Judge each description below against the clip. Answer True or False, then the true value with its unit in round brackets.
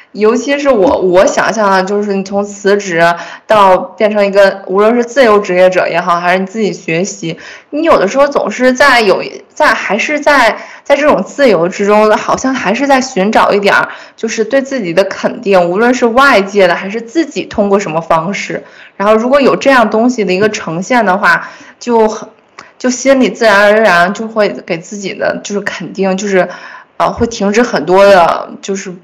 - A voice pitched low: False (205 Hz)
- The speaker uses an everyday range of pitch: True (3.9 semitones)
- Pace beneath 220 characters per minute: False (280 characters per minute)